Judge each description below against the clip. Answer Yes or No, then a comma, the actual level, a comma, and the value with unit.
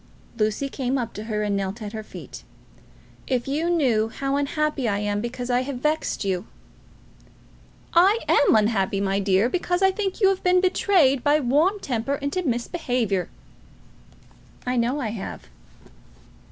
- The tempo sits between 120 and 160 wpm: Yes, average, 155 wpm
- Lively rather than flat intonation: Yes, wide, 6.0 semitones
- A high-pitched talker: Yes, very high, 255 Hz